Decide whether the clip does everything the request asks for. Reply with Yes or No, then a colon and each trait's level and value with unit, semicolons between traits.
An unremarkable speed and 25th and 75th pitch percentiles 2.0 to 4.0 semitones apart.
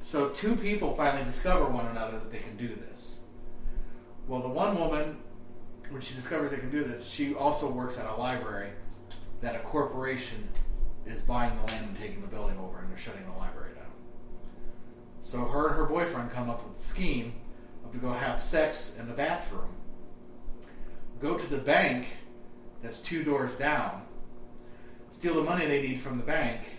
Yes: average, 180 wpm; average, 3.1 semitones